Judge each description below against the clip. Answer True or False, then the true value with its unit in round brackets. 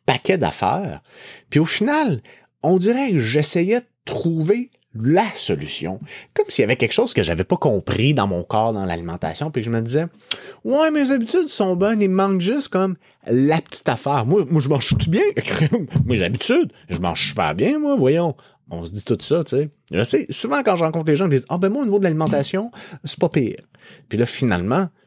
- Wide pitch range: True (6.6 semitones)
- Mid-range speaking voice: True (170 Hz)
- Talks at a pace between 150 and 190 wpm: False (210 wpm)